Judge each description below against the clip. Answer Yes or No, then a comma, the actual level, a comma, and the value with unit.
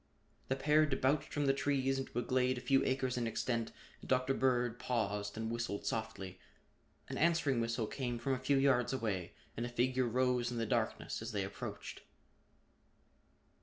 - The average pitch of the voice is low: Yes, low, 125 Hz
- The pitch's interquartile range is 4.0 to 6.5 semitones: No, narrow, 2.5 semitones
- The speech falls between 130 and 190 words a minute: Yes, average, 175 wpm